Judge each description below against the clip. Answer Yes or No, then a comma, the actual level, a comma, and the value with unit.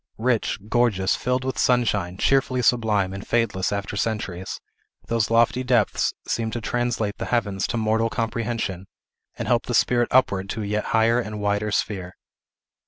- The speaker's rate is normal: Yes, average, 160 wpm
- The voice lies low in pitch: Yes, low, 110 Hz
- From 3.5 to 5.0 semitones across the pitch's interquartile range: No, average, 2.9 semitones